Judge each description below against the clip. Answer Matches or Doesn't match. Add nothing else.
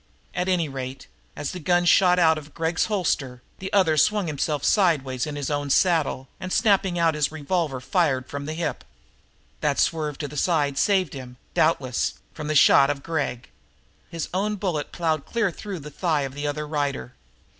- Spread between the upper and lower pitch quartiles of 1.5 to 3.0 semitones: Doesn't match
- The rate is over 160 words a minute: Matches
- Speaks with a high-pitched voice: Doesn't match